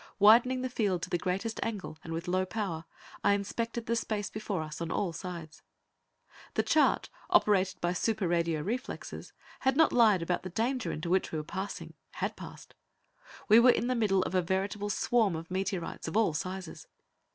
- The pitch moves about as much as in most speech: Yes, average, 4.4 semitones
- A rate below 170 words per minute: No, average, 185 wpm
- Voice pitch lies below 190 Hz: No, high, 195 Hz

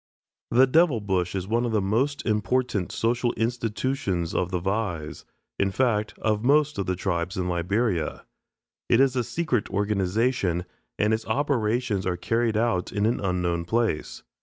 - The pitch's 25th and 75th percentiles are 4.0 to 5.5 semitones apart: Yes, average, 4.6 semitones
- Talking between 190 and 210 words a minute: No, average, 160 wpm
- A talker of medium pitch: No, low, 105 Hz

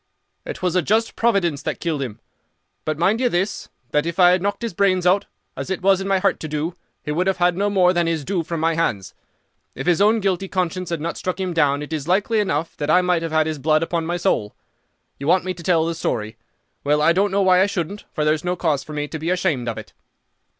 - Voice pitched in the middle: Yes, medium, 175 Hz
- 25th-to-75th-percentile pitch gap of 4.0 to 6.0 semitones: No, average, 3.4 semitones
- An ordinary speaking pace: No, fast, 260 wpm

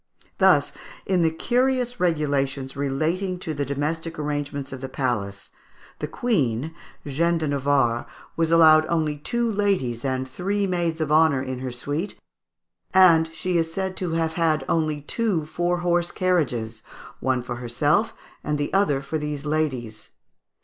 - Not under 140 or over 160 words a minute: Yes, average, 150 wpm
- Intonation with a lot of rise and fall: No, average, 4.2 semitones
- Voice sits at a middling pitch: Yes, medium, 155 Hz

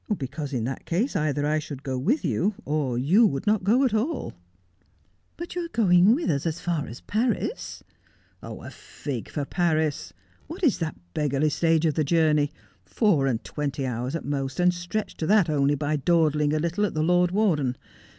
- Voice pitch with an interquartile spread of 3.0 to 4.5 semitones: No, wide, 5.5 semitones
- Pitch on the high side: No, medium, 155 Hz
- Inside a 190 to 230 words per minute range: Yes, average, 200 wpm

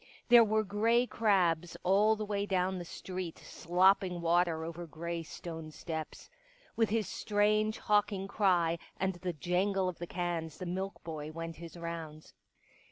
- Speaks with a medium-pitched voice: Yes, medium, 180 Hz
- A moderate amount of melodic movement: Yes, average, 3.4 semitones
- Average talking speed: Yes, average, 155 wpm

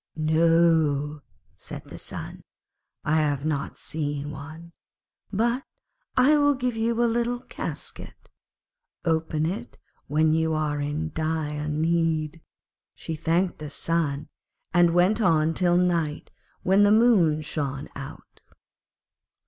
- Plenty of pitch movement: No, average, 3.2 semitones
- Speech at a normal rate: No, slow, 120 wpm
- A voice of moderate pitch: Yes, medium, 160 Hz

